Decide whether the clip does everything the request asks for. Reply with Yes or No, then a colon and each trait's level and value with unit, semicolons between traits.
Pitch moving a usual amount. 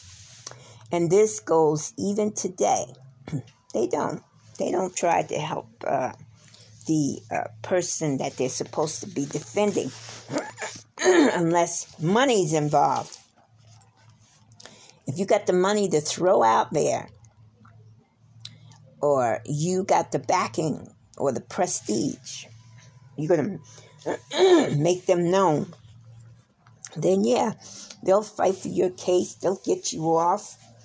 No: wide, 7.3 semitones